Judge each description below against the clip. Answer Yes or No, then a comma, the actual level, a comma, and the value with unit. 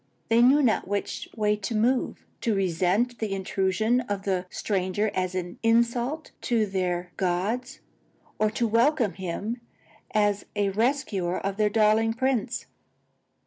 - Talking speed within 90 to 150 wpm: Yes, average, 140 wpm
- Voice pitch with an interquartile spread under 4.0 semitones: Yes, average, 3.6 semitones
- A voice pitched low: No, high, 210 Hz